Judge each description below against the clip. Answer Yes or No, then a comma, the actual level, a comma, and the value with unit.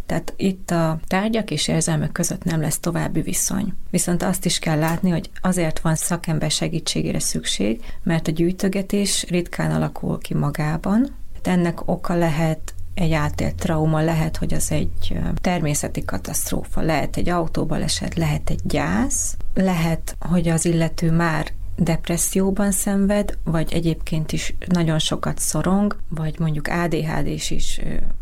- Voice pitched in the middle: Yes, medium, 165 Hz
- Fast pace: No, average, 140 wpm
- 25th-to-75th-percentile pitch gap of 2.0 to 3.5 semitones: Yes, narrow, 2.5 semitones